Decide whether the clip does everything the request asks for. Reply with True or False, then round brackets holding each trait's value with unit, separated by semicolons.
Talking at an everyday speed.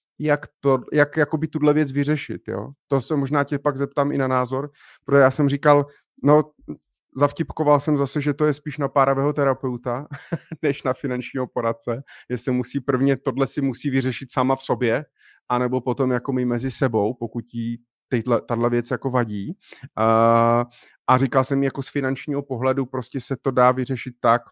False (175 wpm)